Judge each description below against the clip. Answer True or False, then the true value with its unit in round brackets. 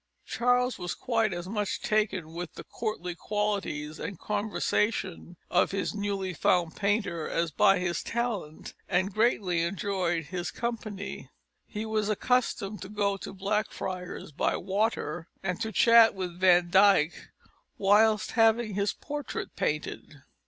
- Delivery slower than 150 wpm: True (135 wpm)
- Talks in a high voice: True (200 Hz)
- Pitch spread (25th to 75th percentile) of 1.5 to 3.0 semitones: False (3.4 semitones)